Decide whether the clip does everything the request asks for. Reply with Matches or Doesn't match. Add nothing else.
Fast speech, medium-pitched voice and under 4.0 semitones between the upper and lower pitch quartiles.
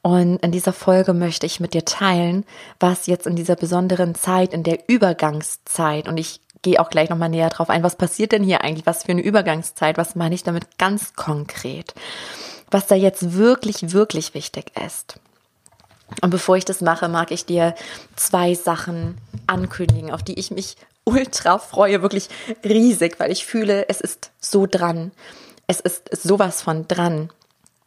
Doesn't match